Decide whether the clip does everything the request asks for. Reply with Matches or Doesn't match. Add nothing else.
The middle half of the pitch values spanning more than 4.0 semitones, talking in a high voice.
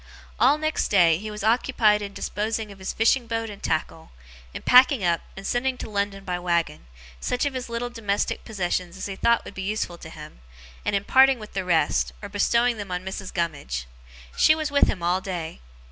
Matches